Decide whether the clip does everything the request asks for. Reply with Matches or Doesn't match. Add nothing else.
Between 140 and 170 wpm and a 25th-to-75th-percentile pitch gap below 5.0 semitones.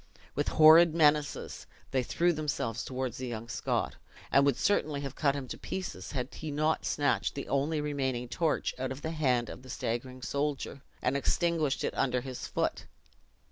Doesn't match